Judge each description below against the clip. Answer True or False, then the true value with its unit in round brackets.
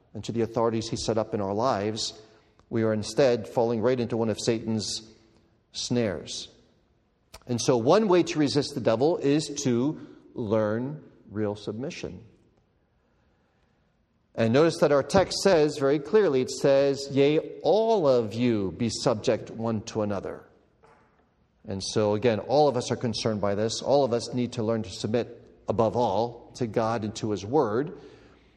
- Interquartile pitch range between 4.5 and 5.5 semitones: False (3.6 semitones)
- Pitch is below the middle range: True (115 Hz)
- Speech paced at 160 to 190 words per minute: True (165 wpm)